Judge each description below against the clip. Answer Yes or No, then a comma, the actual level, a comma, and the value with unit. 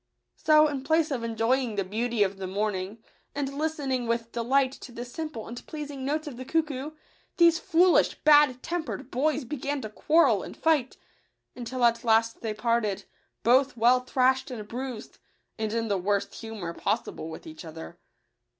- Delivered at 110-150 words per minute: No, average, 170 wpm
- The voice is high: Yes, high, 245 Hz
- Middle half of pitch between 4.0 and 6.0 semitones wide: Yes, average, 4.5 semitones